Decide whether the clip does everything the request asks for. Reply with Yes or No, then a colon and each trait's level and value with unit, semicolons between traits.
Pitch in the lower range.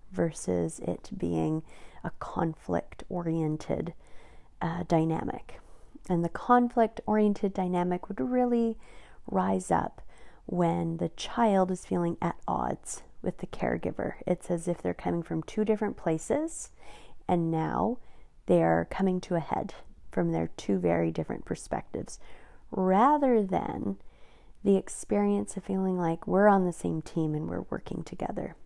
No: medium, 175 Hz